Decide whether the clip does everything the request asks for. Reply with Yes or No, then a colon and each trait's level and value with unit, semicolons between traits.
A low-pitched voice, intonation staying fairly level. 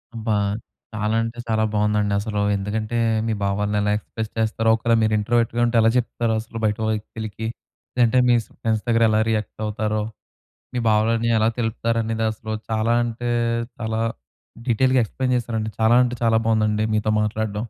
Yes: low, 110 Hz; narrow, 1.3 semitones